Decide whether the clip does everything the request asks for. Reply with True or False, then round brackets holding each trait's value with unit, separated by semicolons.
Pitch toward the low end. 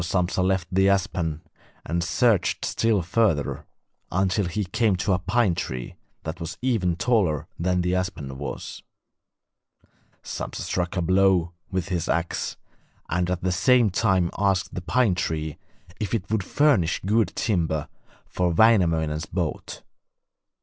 True (90 Hz)